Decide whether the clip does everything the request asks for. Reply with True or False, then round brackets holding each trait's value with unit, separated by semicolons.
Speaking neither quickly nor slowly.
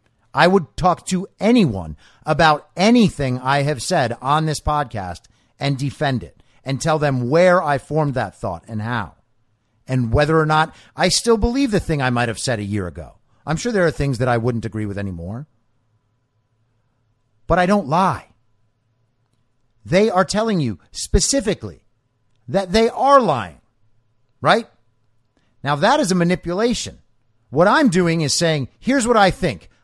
True (165 wpm)